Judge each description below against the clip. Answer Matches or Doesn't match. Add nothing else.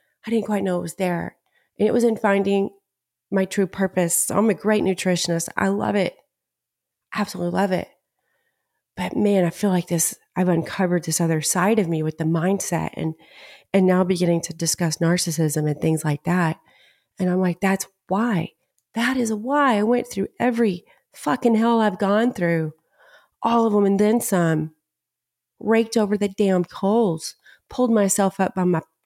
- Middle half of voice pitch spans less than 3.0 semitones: Doesn't match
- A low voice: Doesn't match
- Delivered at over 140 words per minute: Matches